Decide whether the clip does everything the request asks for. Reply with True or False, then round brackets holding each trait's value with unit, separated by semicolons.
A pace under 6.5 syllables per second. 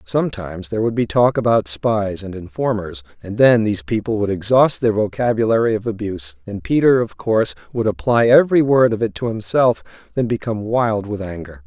True (5.6 syllables/s)